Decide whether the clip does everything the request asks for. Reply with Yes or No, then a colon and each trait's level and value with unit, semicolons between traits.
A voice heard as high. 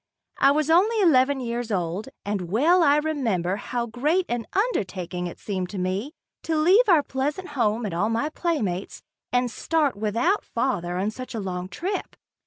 Yes: high, 245 Hz